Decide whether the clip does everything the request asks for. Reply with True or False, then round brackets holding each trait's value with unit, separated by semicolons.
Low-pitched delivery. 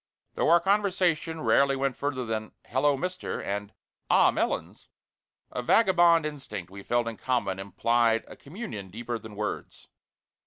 True (130 Hz)